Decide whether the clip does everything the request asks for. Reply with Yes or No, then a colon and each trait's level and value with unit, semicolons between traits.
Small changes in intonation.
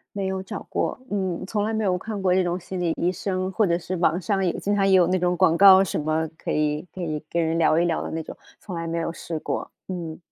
Yes: narrow, 2.3 semitones